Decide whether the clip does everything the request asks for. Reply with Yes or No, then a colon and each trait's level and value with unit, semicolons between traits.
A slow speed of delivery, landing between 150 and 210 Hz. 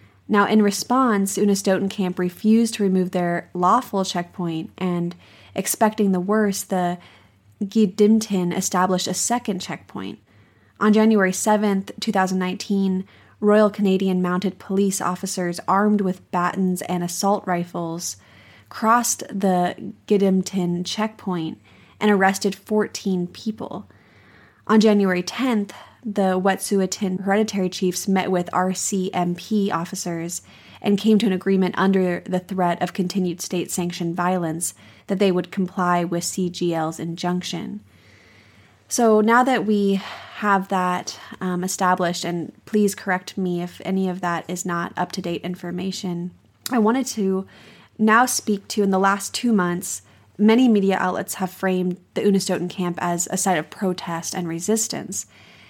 Yes: slow, 130 wpm; medium, 185 Hz